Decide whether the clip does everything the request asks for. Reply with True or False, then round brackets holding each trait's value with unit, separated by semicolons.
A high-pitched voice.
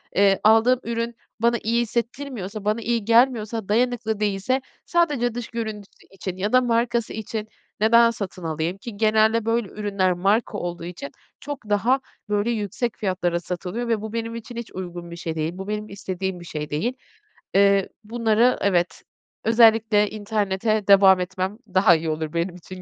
True (210 Hz)